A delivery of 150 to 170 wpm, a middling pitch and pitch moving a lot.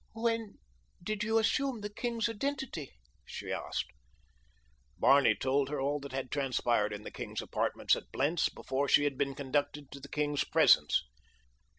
Yes: average, 160 wpm; medium, 145 Hz; wide, 7.8 semitones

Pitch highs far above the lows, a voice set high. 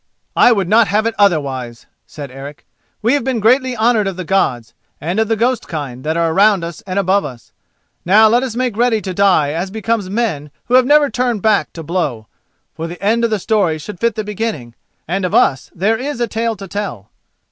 Yes: wide, 5.7 semitones; high, 200 Hz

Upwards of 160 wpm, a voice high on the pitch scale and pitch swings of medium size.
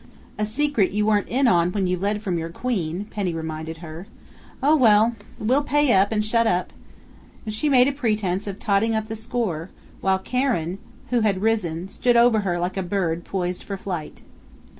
Yes: average, 190 wpm; high, 205 Hz; average, 4.2 semitones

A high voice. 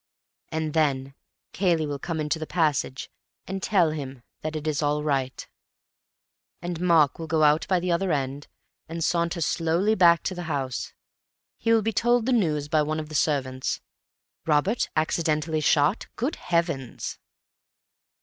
No: medium, 155 Hz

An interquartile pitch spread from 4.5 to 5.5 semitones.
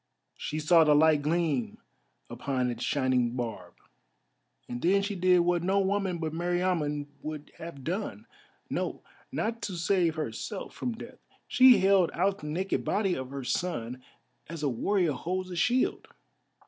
Yes: average, 4.8 semitones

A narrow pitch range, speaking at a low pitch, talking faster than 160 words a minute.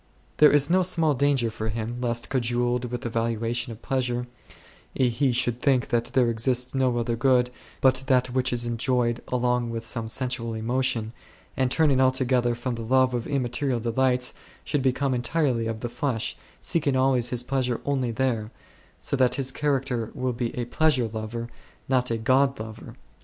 Yes: narrow, 2.1 semitones; low, 125 Hz; average, 180 wpm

